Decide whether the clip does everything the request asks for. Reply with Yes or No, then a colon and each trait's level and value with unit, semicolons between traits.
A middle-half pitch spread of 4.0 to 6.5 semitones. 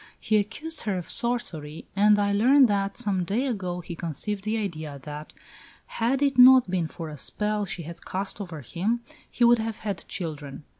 Yes: average, 4.9 semitones